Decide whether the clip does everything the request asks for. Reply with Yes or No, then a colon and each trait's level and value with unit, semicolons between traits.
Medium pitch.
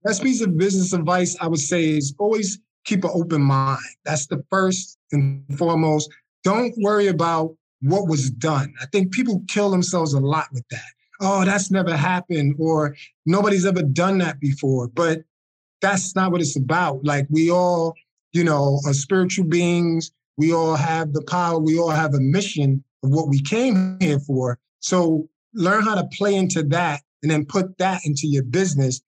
Yes: medium, 165 Hz